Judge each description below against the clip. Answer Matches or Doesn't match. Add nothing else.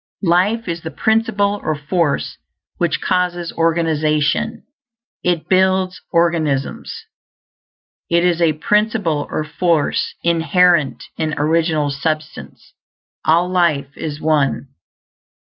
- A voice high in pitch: Doesn't match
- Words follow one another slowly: Matches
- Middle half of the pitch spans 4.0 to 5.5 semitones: Doesn't match